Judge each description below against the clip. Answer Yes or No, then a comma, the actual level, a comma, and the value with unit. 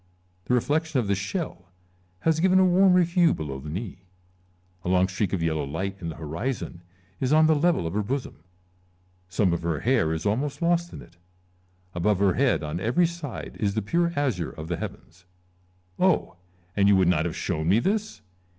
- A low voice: Yes, low, 105 Hz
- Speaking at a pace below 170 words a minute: No, average, 195 wpm